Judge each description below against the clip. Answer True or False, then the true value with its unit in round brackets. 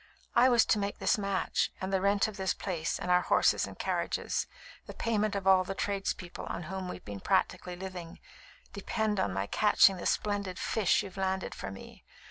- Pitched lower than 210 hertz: True (190 Hz)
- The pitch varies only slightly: True (2.1 semitones)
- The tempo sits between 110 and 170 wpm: False (195 wpm)